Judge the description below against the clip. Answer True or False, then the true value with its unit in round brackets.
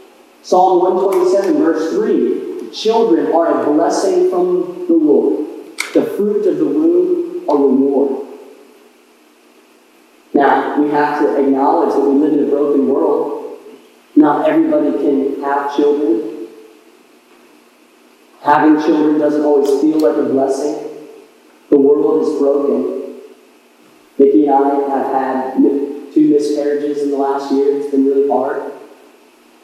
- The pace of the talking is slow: True (125 wpm)